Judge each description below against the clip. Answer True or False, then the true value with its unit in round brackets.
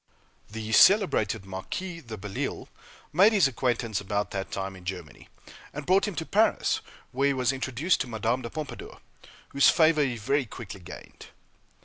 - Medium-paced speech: True (160 wpm)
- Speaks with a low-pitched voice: True (125 Hz)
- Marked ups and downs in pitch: True (7.3 semitones)